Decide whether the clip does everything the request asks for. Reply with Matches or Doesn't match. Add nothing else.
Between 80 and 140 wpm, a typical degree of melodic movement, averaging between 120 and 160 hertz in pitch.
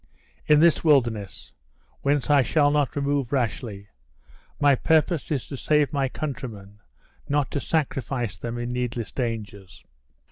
Matches